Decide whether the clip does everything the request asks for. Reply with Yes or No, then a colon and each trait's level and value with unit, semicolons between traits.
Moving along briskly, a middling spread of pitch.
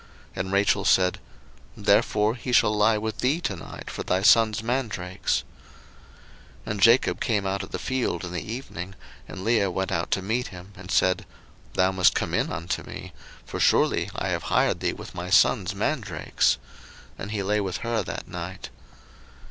No: average, 180 wpm; average, 3.2 semitones